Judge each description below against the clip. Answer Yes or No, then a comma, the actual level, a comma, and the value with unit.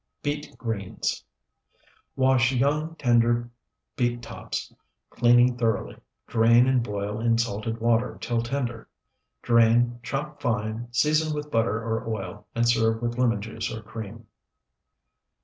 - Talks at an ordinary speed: No, slow, 125 wpm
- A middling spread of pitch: No, narrow, 1.6 semitones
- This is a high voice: No, low, 120 Hz